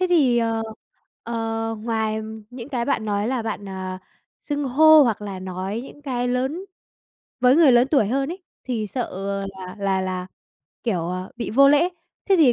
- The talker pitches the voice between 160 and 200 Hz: No, high, 230 Hz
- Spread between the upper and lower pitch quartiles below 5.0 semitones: No, average, 5.3 semitones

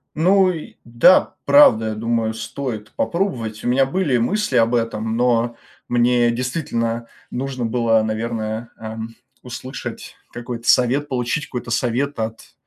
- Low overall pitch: Yes, low, 120 Hz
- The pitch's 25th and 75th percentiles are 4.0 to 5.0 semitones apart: No, average, 2.7 semitones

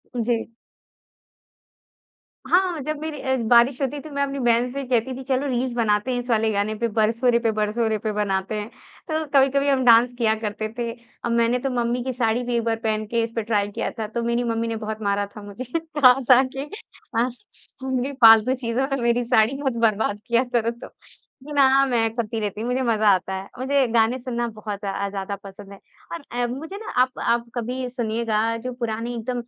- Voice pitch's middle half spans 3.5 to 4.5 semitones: No, average, 2.7 semitones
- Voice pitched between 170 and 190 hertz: No, high, 235 Hz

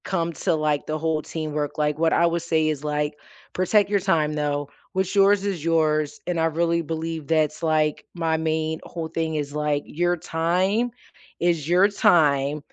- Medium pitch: Yes, medium, 160 Hz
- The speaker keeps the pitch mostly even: Yes, narrow, 2.1 semitones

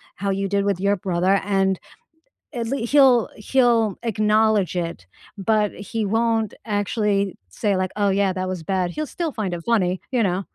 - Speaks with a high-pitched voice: Yes, high, 200 Hz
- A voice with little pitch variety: No, average, 3.0 semitones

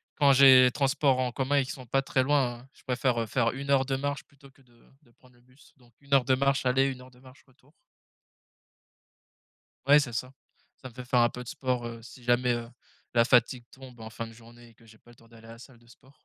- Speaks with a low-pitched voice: Yes, low, 125 Hz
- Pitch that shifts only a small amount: Yes, narrow, 2.1 semitones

